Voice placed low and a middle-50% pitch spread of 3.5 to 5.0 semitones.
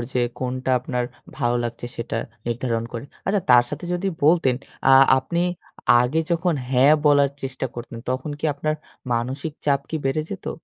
Yes: low, 130 Hz; average, 3.8 semitones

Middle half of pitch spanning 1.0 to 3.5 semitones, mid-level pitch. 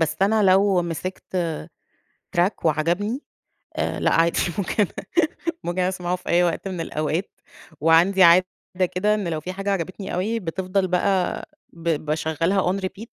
Yes: average, 2.7 semitones; medium, 180 Hz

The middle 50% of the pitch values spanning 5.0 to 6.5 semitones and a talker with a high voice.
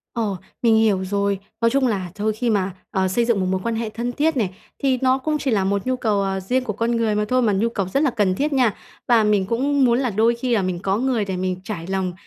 No: average, 4.2 semitones; high, 220 Hz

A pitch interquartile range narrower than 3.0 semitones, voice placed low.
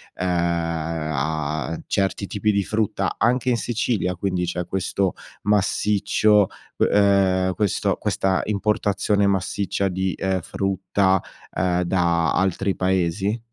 Yes: narrow, 2.4 semitones; very low, 95 Hz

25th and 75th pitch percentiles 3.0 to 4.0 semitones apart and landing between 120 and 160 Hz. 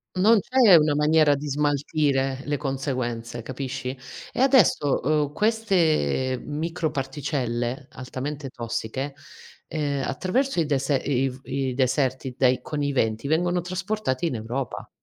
Yes: average, 3.4 semitones; medium, 140 Hz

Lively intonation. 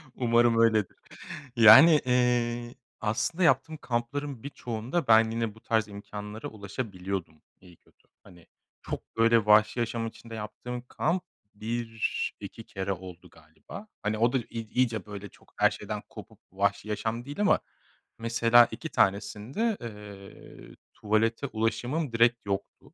No: average, 2.7 semitones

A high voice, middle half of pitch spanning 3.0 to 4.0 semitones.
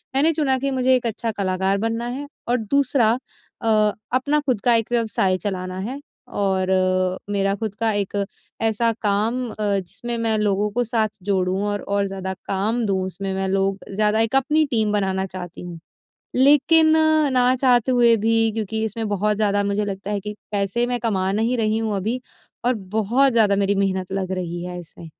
Yes: high, 210 Hz; average, 3.5 semitones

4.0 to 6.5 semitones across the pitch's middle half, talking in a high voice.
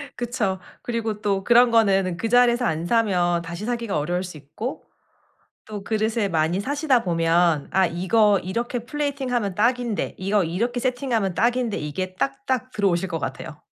Yes: average, 5.2 semitones; high, 210 Hz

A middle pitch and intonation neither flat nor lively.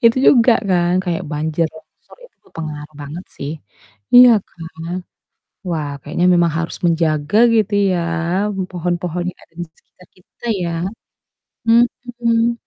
No: medium, 175 Hz; wide, 6.1 semitones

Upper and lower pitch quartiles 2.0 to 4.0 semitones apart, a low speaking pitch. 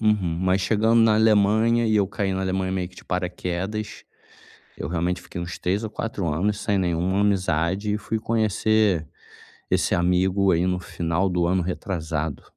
Yes: average, 3.1 semitones; very low, 95 Hz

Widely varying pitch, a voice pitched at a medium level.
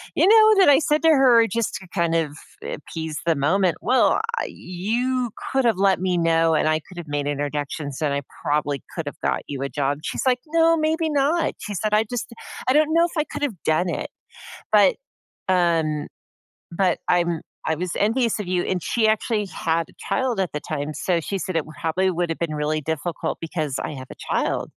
Yes: wide, 7.4 semitones; medium, 180 Hz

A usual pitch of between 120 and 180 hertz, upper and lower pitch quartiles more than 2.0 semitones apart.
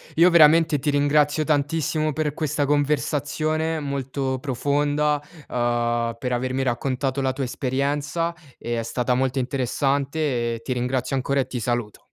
Yes: medium, 140 Hz; average, 2.8 semitones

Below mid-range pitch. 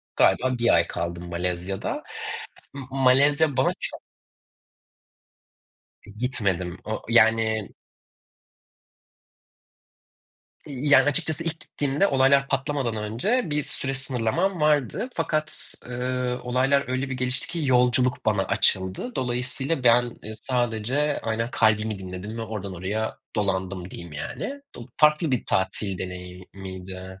Yes: low, 120 Hz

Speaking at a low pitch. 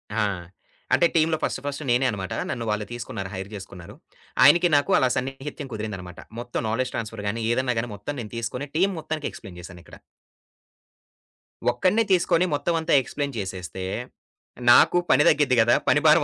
Yes: low, 125 Hz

